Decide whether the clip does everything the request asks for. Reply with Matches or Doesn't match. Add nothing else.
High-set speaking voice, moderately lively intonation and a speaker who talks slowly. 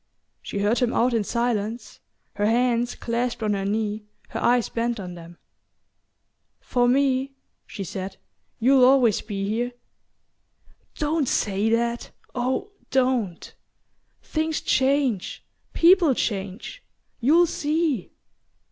Matches